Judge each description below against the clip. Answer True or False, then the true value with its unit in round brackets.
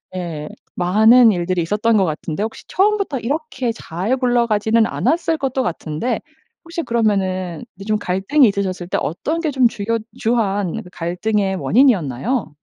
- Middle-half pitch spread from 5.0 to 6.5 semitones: True (5.5 semitones)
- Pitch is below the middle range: False (215 Hz)